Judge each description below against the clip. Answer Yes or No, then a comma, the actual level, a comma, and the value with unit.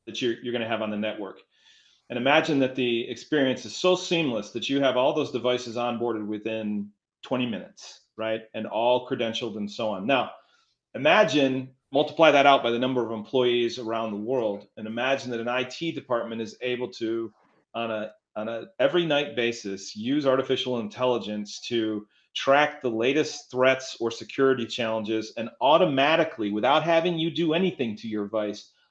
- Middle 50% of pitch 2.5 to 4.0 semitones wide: Yes, average, 3.5 semitones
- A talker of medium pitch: No, low, 120 Hz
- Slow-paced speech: No, average, 175 wpm